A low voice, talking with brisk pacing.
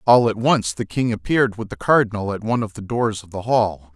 Yes: low, 110 Hz; fast, 260 wpm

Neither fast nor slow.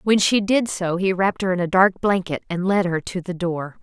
No: fast, 265 wpm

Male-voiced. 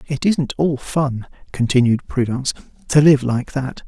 Yes: male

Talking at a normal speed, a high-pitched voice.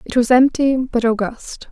Yes: average, 175 wpm; high, 245 Hz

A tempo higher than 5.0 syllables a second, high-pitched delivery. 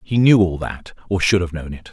No: 5.4 syllables/s; very low, 90 Hz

